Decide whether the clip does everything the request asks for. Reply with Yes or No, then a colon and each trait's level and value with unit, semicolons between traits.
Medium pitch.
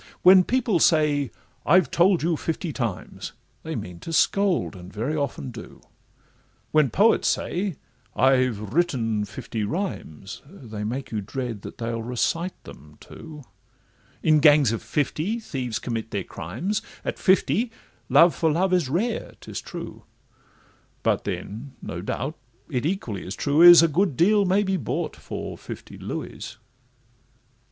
Yes: medium, 145 Hz